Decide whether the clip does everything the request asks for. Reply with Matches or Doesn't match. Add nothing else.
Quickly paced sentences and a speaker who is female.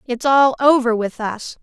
Doesn't match